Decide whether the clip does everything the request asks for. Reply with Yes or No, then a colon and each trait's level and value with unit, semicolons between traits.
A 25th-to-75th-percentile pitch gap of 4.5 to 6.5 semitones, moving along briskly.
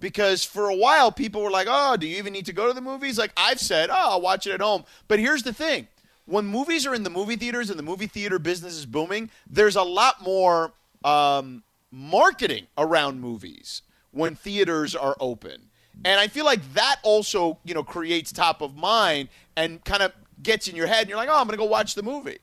Yes: average, 5.2 semitones; fast, 225 wpm